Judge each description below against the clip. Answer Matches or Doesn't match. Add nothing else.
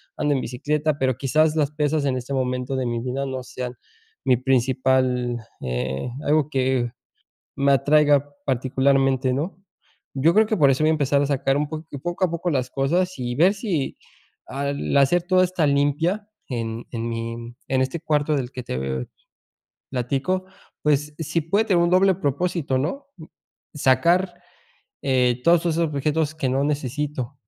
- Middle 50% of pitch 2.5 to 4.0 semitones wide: Matches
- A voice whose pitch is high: Doesn't match